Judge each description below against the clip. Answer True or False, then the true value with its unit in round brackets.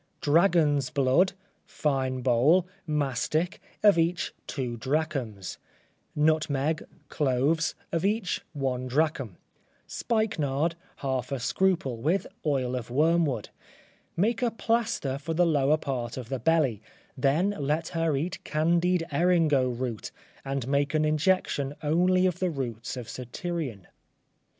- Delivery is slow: True (120 wpm)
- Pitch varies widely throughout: False (4.4 semitones)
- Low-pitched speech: False (150 Hz)